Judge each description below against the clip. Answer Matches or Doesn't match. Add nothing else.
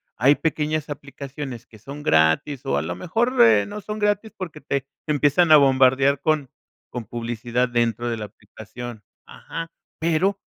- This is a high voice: Doesn't match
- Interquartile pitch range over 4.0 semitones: Matches